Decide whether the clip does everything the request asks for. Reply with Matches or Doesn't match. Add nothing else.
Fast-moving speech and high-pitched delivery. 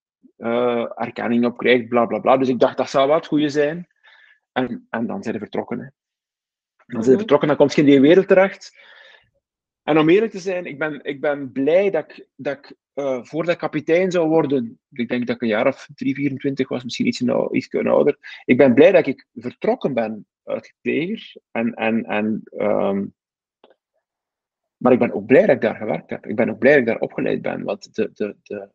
Doesn't match